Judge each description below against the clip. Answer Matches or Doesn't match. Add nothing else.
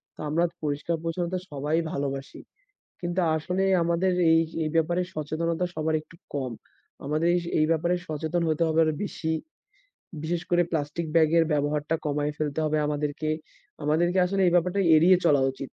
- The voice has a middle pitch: Matches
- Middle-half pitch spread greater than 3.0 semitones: Doesn't match